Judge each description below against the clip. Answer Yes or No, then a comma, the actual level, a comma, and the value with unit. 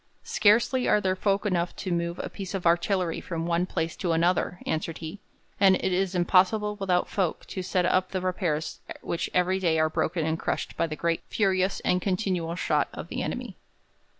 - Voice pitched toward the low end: No, medium, 180 Hz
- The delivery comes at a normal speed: Yes, average, 195 wpm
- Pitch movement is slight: Yes, narrow, 2.2 semitones